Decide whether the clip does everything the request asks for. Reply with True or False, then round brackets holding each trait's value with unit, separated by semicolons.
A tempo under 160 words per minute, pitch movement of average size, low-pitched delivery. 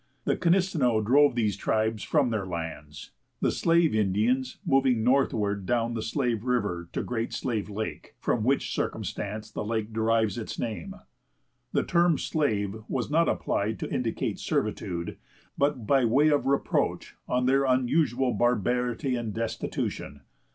True (145 wpm; 3.9 semitones; 120 Hz)